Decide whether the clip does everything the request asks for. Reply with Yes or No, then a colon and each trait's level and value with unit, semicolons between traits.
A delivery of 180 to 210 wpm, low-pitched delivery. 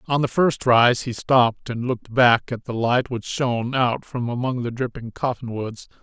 Yes: average, 200 wpm; low, 120 Hz